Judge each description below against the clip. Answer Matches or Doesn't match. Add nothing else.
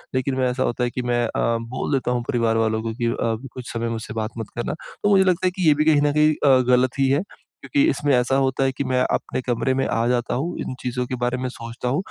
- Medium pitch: Doesn't match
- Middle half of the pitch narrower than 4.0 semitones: Matches